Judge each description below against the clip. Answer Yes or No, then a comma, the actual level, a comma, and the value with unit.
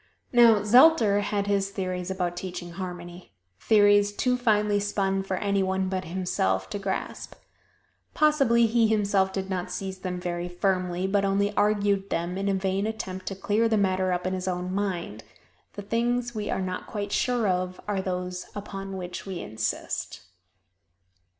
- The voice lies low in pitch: No, high, 195 Hz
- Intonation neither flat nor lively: No, narrow, 2.0 semitones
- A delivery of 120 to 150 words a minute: No, average, 165 wpm